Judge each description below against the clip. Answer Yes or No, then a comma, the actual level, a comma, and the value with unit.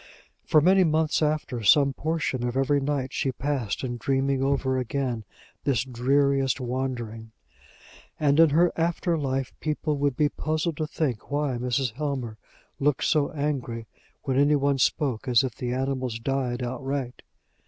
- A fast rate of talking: No, average, 155 wpm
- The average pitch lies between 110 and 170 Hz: Yes, low, 135 Hz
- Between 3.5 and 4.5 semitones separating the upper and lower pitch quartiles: No, average, 2.8 semitones